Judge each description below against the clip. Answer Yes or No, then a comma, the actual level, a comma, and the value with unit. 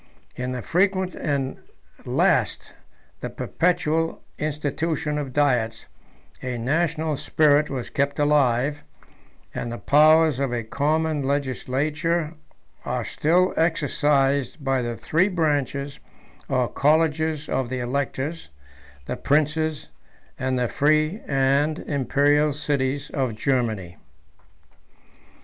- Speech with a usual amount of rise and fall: Yes, average, 3.0 semitones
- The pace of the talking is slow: Yes, slow, 110 wpm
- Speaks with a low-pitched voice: No, medium, 145 Hz